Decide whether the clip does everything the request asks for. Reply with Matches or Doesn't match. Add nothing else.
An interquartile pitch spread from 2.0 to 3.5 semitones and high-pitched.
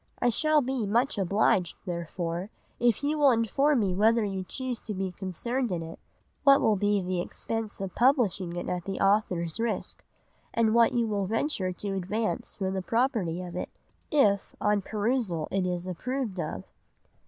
Doesn't match